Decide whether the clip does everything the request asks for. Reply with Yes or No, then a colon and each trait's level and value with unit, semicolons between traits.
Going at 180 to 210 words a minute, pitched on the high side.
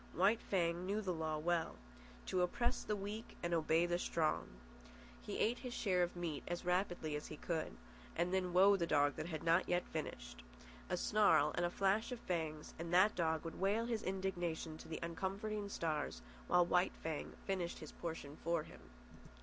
No: average, 190 wpm; medium, 175 Hz